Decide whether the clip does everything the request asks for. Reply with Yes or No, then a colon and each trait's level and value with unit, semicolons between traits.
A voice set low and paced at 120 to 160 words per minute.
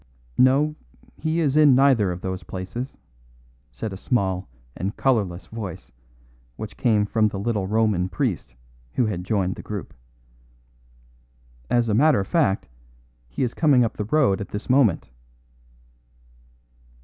Yes: low, 110 Hz; average, 140 wpm